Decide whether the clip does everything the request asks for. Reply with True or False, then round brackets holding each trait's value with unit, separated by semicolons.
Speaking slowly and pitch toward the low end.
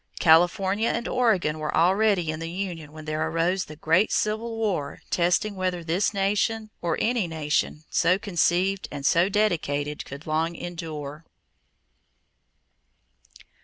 False (130 wpm; 175 Hz)